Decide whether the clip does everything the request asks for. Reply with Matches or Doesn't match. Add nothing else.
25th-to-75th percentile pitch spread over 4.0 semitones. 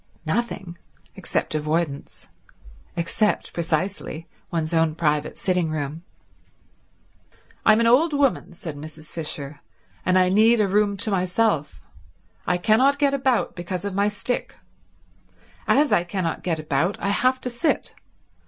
Matches